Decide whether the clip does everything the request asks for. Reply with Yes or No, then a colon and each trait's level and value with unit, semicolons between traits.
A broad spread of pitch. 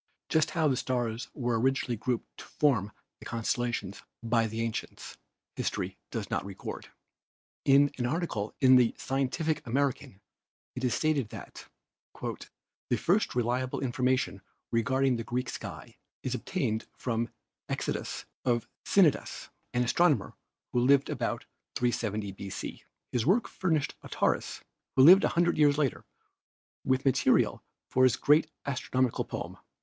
No: average, 3.4 semitones